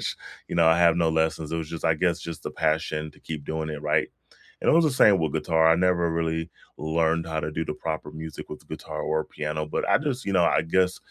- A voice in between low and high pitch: No, very low, 80 Hz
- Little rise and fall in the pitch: Yes, narrow, 1.5 semitones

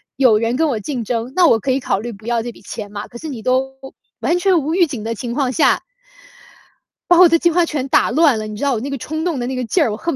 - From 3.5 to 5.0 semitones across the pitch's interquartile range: No, wide, 5.5 semitones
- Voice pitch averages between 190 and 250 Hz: No, very high, 260 Hz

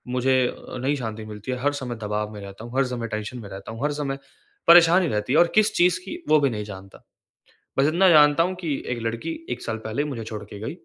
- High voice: No, low, 125 Hz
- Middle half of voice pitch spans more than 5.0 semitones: Yes, wide, 5.5 semitones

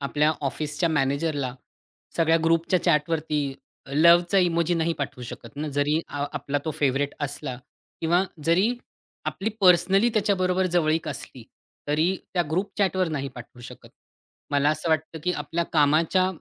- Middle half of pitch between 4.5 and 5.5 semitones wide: No, average, 3.4 semitones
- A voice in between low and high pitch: Yes, medium, 160 Hz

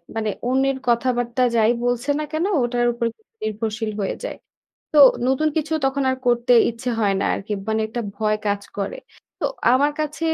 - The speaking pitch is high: Yes, high, 240 Hz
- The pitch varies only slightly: No, average, 3.4 semitones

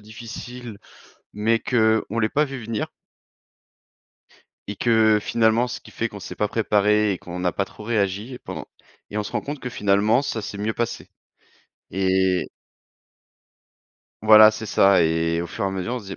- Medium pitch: No, low, 105 Hz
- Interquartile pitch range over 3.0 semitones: No, narrow, 2.6 semitones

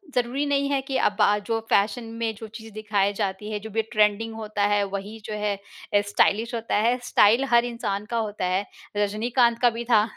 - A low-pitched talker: No, high, 215 Hz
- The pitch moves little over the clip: Yes, narrow, 2.3 semitones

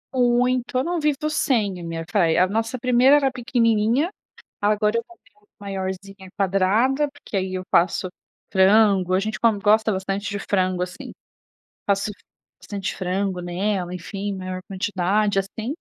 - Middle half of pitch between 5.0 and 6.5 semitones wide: No, average, 3.6 semitones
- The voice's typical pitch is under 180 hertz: No, high, 205 Hz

